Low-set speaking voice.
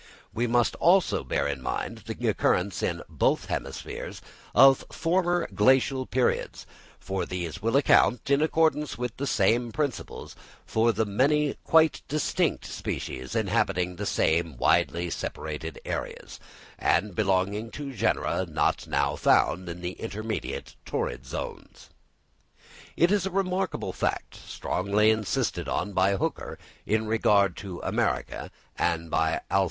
Yes: low, 110 Hz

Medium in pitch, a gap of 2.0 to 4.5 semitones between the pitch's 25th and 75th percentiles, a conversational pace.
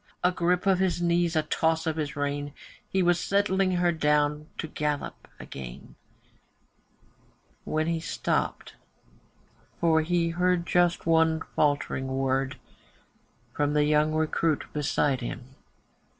No: medium, 160 Hz; average, 2.9 semitones; slow, 130 wpm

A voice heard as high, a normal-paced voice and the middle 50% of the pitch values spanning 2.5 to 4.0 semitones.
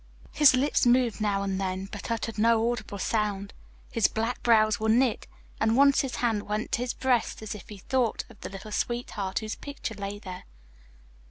Yes: high, 220 Hz; average, 190 wpm; average, 2.9 semitones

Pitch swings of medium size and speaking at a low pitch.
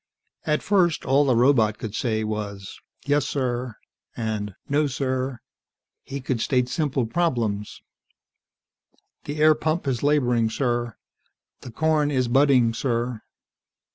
Yes: average, 3.9 semitones; low, 130 Hz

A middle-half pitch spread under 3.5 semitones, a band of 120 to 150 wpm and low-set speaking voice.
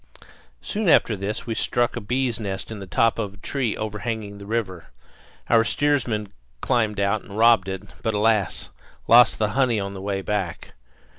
No: average, 2.8 semitones; average, 175 wpm; low, 110 Hz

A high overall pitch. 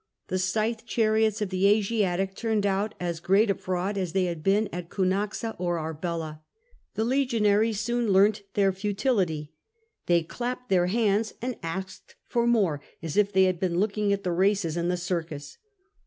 Yes: high, 195 Hz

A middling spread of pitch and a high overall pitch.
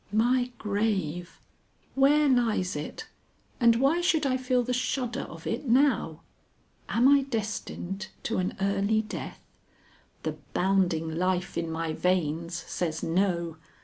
No: wide, 6.4 semitones; high, 200 Hz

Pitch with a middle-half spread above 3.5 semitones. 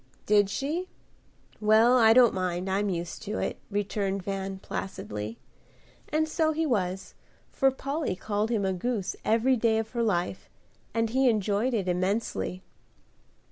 Yes: average, 4.1 semitones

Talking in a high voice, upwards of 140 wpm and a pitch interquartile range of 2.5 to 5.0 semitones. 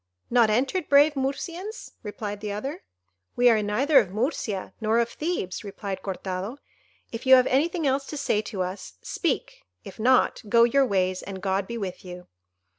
No: high, 230 Hz; average, 175 wpm; wide, 5.5 semitones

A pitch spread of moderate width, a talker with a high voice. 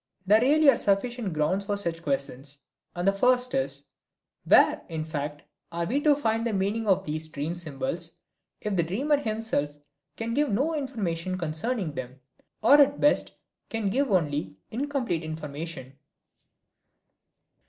No: wide, 7.8 semitones; high, 195 Hz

